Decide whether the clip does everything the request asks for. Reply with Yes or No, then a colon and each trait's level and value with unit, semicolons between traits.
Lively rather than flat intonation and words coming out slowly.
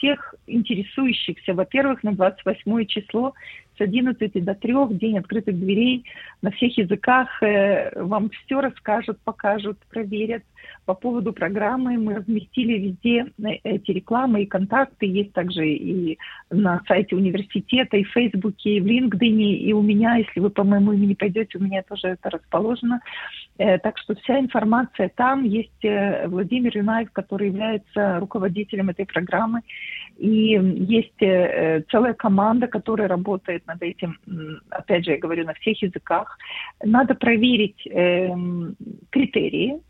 No: average, 3.3 semitones; slow, 130 wpm